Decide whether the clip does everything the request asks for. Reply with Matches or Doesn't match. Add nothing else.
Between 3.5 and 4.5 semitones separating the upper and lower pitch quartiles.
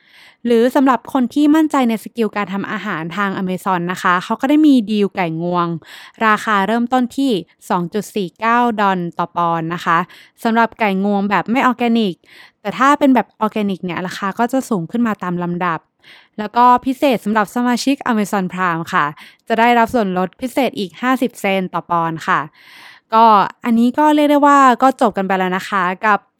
Doesn't match